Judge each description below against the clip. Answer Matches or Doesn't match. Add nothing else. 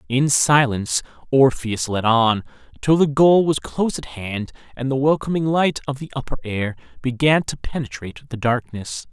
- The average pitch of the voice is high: Doesn't match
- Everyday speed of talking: Matches